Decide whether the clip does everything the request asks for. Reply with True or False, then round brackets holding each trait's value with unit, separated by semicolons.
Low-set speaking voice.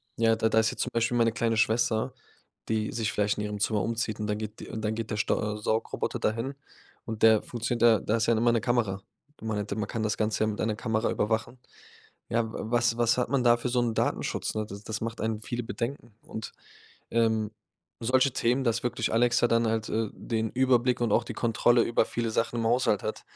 True (115 Hz)